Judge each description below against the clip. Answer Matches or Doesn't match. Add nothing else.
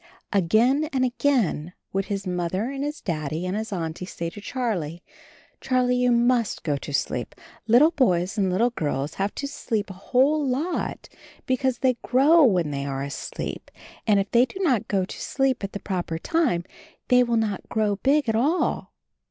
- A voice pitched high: Matches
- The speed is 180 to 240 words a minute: Matches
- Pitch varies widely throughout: Matches